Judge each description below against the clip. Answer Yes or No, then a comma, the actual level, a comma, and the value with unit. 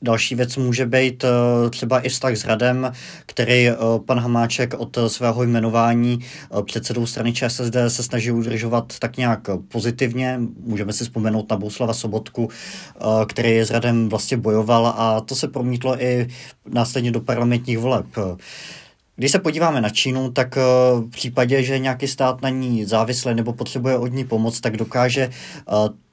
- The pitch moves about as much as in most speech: No, narrow, 1.9 semitones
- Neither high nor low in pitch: No, low, 120 Hz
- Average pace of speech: Yes, average, 150 wpm